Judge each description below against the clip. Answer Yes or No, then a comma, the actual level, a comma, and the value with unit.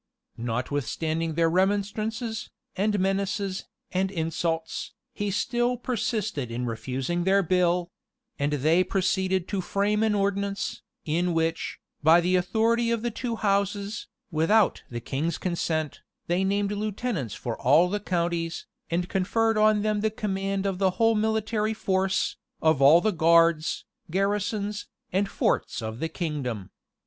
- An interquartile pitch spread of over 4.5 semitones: No, average, 4.1 semitones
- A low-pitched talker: No, high, 190 Hz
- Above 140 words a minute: No, slow, 135 wpm